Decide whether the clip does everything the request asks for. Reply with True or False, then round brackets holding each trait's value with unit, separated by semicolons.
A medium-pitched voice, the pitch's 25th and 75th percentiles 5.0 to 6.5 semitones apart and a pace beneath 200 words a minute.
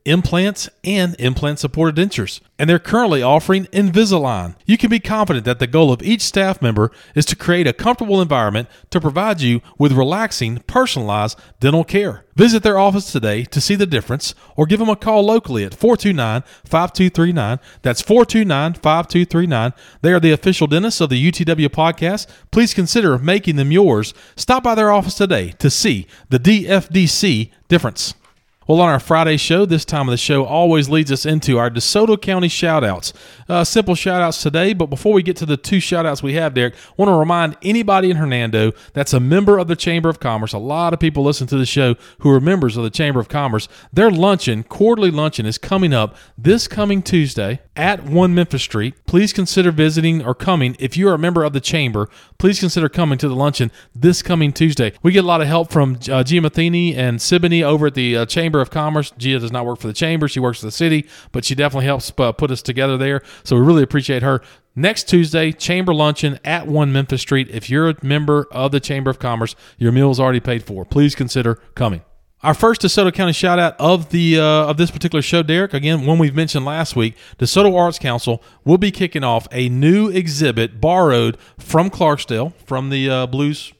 False (155 Hz; 5.6 semitones; 205 wpm)